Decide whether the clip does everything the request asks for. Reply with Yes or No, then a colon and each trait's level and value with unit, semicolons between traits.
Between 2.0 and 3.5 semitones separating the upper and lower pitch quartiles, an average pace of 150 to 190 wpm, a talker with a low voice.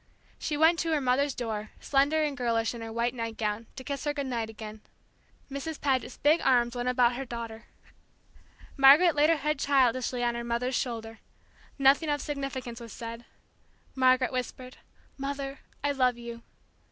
No: average, 3.1 semitones; average, 165 wpm; very high, 255 Hz